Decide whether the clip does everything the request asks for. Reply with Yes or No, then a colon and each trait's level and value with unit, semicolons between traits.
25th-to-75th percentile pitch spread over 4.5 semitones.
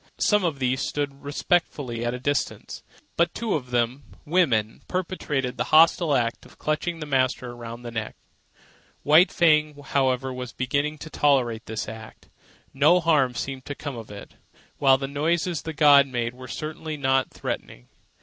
No: average, 3.7 semitones